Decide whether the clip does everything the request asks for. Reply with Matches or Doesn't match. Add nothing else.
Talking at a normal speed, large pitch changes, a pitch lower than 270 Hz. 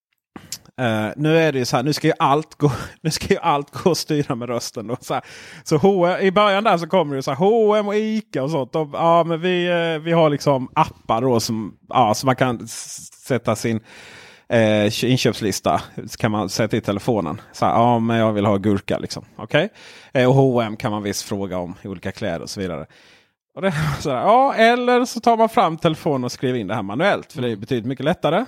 Doesn't match